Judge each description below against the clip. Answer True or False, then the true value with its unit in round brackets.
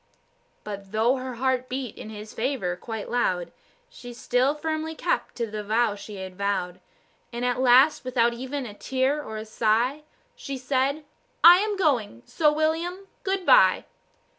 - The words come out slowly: False (155 wpm)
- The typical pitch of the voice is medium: False (250 Hz)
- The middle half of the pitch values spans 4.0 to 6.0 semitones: True (5.4 semitones)